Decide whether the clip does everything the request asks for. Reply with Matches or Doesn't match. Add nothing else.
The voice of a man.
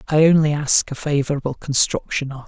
Matches